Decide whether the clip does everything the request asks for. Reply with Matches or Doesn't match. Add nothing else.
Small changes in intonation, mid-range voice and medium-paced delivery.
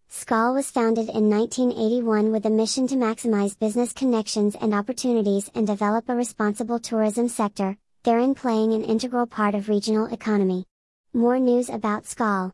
Doesn't match